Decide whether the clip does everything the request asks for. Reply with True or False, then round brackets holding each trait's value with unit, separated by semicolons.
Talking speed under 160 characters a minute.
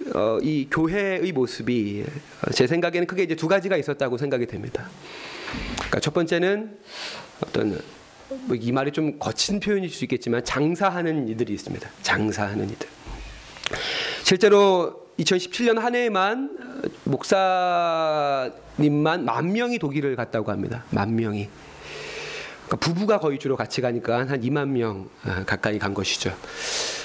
False (280 characters per minute)